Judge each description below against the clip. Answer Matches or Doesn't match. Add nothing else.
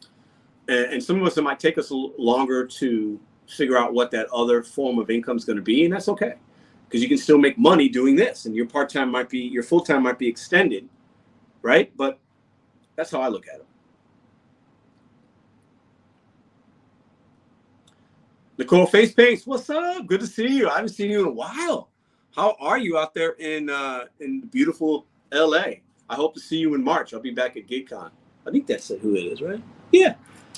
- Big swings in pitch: Matches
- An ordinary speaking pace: Matches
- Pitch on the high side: Doesn't match